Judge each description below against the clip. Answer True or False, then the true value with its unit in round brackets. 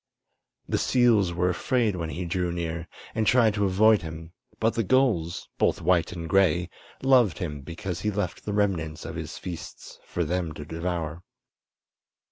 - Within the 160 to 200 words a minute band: True (165 wpm)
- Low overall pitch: True (90 Hz)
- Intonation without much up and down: False (3.8 semitones)